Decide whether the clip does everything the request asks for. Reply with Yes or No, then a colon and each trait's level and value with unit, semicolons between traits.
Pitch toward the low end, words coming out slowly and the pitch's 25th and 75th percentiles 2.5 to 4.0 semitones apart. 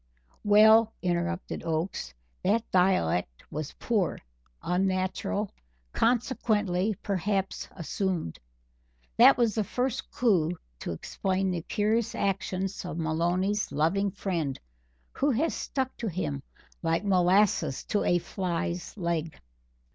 No: medium, 185 Hz; slow, 110 wpm; average, 3.6 semitones